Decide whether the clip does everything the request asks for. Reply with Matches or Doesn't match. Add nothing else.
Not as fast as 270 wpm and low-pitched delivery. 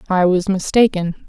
Doesn't match